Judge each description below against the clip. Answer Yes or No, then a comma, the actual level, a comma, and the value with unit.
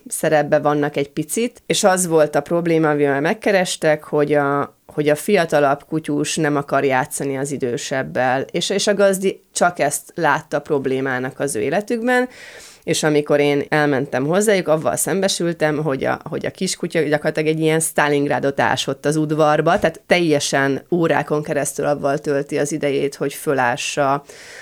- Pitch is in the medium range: Yes, medium, 150 Hz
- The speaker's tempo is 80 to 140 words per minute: No, average, 150 wpm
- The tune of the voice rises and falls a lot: No, narrow, 2.6 semitones